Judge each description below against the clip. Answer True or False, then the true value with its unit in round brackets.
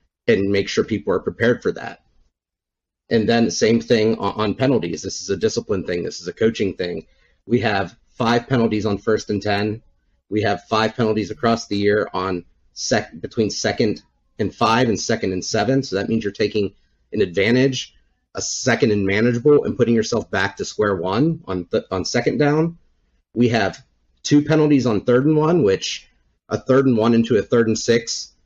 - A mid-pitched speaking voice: False (110 Hz)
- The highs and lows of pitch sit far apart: False (4.1 semitones)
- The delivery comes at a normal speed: True (190 wpm)